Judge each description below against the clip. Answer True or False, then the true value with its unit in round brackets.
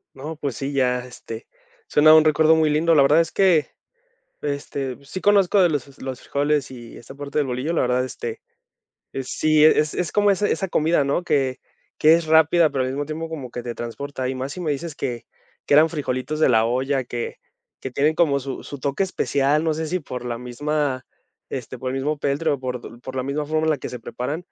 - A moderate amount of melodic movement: True (3.4 semitones)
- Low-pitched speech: False (145 Hz)